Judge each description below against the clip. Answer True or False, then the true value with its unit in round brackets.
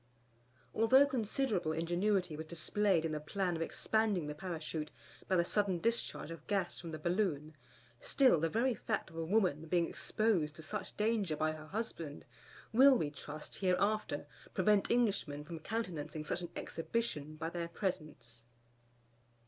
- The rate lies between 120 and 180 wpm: True (155 wpm)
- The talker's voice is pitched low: False (175 Hz)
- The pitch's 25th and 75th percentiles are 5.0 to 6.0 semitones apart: True (5.3 semitones)